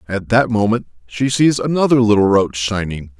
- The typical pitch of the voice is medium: No, low, 110 Hz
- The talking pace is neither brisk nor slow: Yes, average, 170 wpm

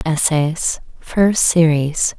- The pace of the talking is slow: Yes, slow, 85 wpm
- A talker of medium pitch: Yes, medium, 160 Hz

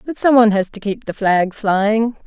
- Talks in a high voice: Yes, high, 215 Hz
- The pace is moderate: No, fast, 240 wpm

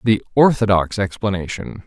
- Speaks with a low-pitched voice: Yes, low, 105 Hz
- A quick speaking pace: No, slow, 95 wpm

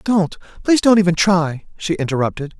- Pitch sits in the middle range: Yes, medium, 175 Hz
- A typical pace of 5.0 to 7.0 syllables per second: Yes, 5.7 syllables/s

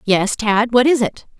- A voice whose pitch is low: No, high, 225 Hz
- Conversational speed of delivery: No, fast, 215 wpm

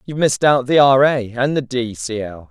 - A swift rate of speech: Yes, fast, 265 wpm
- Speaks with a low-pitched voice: Yes, low, 125 Hz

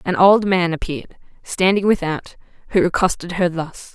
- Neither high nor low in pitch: Yes, medium, 175 Hz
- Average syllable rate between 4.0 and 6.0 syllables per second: Yes, 5.0 syllables/s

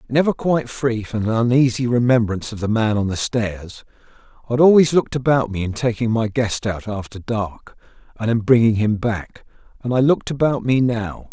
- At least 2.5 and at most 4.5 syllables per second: No, 5.3 syllables/s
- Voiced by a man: Yes, male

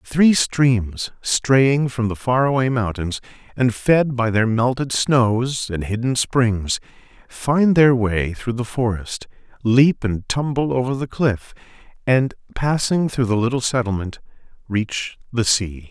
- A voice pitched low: Yes, low, 120 Hz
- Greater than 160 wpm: No, average, 145 wpm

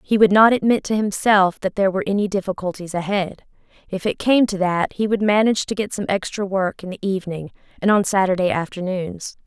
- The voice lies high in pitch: Yes, high, 195 Hz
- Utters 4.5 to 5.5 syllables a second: No, 5.9 syllables/s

